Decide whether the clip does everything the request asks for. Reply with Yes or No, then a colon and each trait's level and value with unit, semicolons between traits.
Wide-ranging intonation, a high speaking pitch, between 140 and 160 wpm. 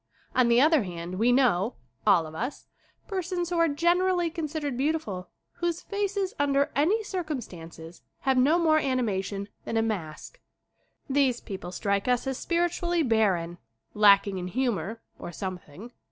Yes: wide, 8.9 semitones; very high, 255 Hz; average, 150 wpm